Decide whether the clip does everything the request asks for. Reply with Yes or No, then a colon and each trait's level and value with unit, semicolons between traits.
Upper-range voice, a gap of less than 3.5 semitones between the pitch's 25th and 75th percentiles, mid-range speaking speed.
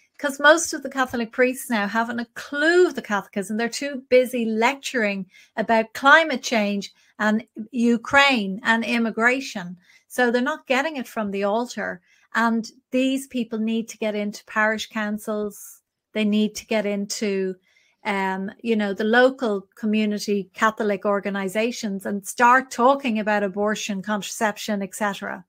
Yes: high, 225 Hz; average, 3.1 semitones; average, 145 wpm